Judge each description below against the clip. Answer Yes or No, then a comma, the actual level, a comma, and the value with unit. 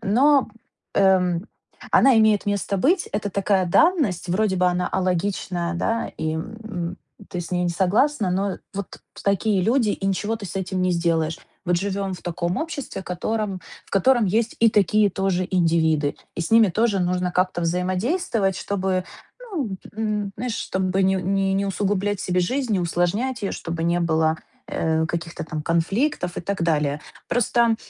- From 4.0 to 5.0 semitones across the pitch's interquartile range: No, average, 3.3 semitones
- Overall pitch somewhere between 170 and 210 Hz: Yes, high, 190 Hz